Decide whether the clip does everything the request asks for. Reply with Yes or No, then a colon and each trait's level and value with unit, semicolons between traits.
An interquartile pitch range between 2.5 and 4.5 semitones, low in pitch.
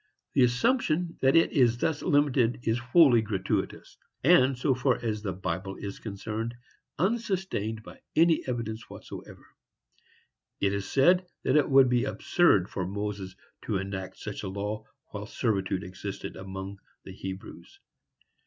No: wide, 5.6 semitones; low, 115 Hz